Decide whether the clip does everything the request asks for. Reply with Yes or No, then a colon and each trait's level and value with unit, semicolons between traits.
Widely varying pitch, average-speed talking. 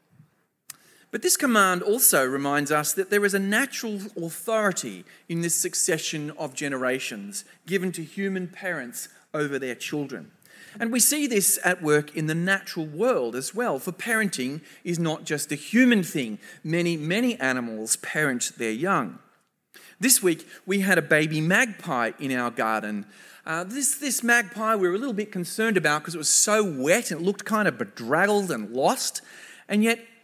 Yes: wide, 5.7 semitones; average, 170 wpm